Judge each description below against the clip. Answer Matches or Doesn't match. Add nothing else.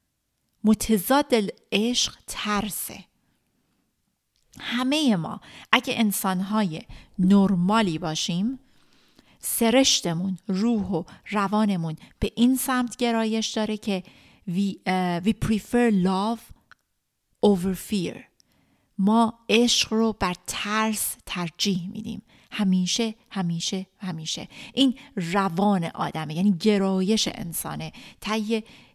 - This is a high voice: Matches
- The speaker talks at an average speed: Doesn't match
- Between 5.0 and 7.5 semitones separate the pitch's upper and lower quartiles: Doesn't match